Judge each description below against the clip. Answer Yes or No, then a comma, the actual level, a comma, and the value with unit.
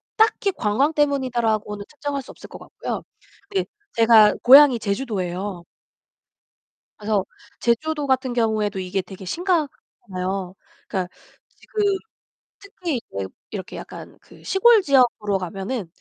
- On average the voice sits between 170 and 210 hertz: No, high, 230 Hz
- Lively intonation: Yes, wide, 6.6 semitones